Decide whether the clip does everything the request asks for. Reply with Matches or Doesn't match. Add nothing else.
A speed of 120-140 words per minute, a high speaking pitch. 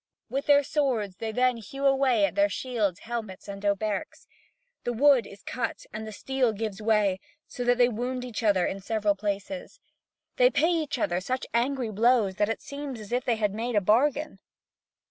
Doesn't match